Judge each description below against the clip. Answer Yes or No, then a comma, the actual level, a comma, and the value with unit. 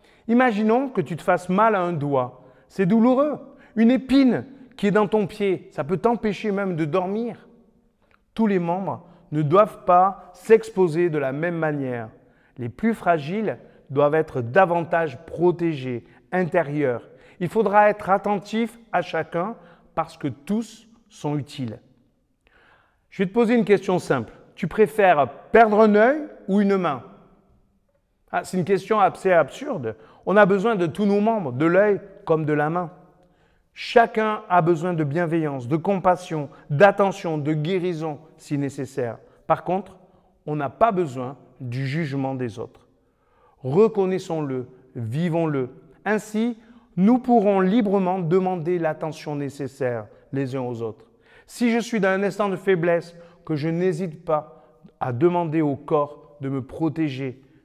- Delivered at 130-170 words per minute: Yes, average, 150 wpm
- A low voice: No, medium, 180 Hz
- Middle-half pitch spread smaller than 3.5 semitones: No, wide, 5.6 semitones